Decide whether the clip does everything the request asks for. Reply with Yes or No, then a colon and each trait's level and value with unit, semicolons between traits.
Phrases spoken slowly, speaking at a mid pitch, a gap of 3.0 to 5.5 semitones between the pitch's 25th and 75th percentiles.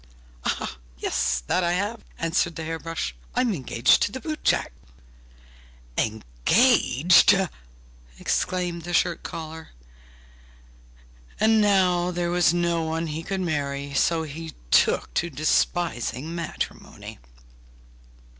No: slow, 110 wpm; medium, 170 Hz; narrow, 2.6 semitones